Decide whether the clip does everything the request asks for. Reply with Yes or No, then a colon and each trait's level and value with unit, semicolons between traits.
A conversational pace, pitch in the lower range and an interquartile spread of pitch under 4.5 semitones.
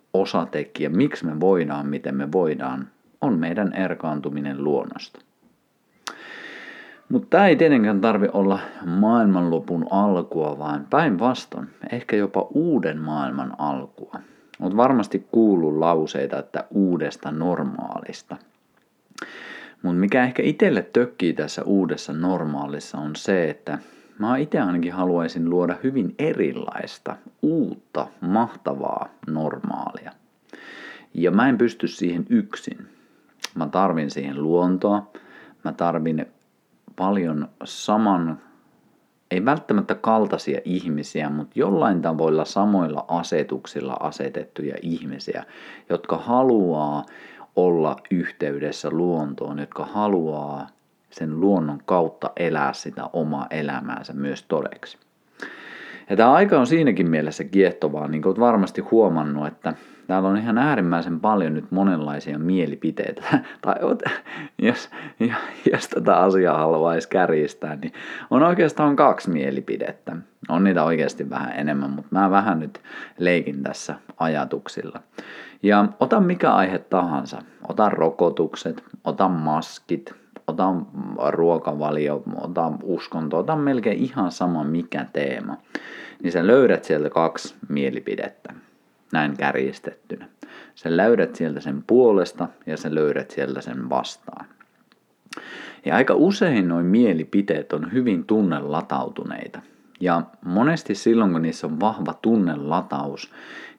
No: average, 115 wpm; very low, 85 Hz; average, 5.3 semitones